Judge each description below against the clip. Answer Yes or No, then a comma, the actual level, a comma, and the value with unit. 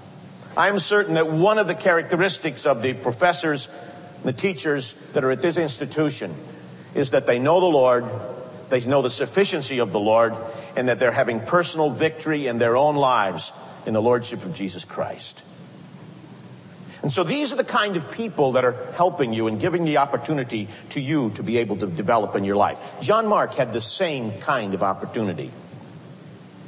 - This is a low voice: No, medium, 145 Hz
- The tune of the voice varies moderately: No, wide, 5.9 semitones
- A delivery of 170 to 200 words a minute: Yes, average, 185 wpm